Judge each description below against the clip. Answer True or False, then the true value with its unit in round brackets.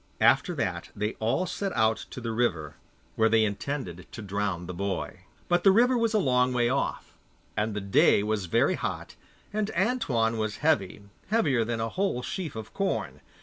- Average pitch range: False (8.7 semitones)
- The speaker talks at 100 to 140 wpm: False (185 wpm)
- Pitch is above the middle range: False (115 Hz)